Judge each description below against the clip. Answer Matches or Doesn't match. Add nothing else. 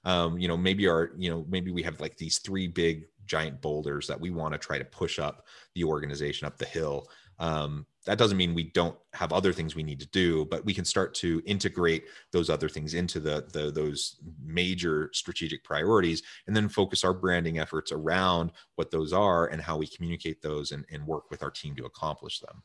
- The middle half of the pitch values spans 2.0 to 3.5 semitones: Matches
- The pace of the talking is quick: Matches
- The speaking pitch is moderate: Doesn't match